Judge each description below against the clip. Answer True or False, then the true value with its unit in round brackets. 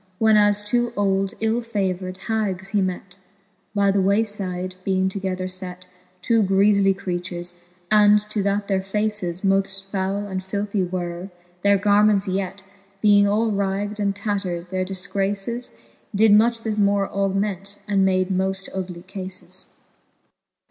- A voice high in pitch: True (195 Hz)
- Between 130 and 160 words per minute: True (140 wpm)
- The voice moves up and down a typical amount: False (1.7 semitones)